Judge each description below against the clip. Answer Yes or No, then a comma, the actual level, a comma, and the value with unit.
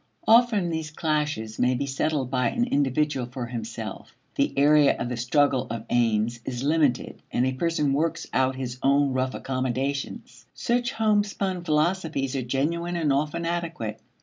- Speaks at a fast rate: No, average, 155 wpm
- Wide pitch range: No, average, 4.6 semitones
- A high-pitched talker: No, medium, 140 Hz